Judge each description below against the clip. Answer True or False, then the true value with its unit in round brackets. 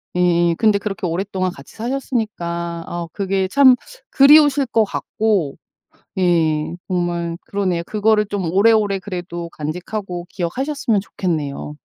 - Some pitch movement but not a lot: True (4.0 semitones)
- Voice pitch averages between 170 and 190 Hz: True (185 Hz)